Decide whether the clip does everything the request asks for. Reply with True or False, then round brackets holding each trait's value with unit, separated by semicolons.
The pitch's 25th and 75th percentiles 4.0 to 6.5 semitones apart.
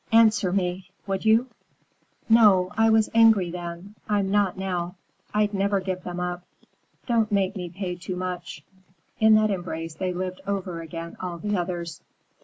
False (2.7 semitones)